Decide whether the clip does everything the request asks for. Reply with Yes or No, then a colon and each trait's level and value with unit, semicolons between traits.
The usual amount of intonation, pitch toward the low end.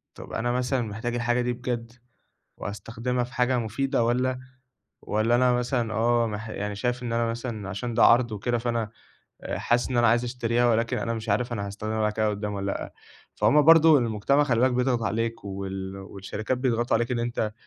No: narrow, 2.3 semitones; low, 115 Hz